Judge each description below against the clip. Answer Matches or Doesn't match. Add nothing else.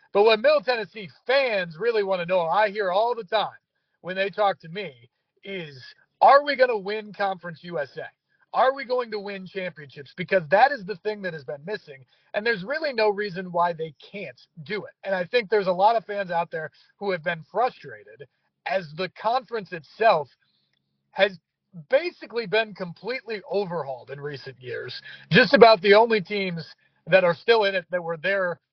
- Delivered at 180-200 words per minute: Matches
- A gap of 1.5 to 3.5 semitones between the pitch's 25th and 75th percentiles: Doesn't match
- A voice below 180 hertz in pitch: Doesn't match